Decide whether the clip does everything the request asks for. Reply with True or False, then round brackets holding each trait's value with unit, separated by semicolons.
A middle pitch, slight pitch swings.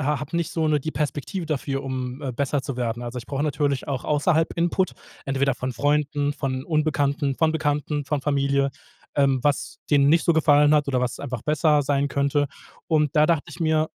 True (145 Hz; 1.9 semitones)